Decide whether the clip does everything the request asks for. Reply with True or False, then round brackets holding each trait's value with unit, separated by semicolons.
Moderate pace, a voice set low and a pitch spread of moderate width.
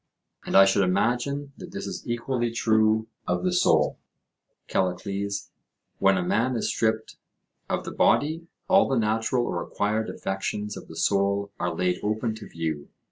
True (160 wpm; 110 Hz; 3.6 semitones)